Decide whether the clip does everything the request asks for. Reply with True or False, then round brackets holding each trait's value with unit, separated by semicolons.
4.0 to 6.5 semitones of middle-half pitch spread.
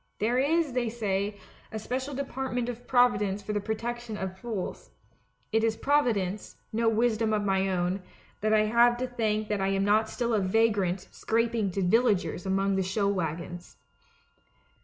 False (3.5 semitones)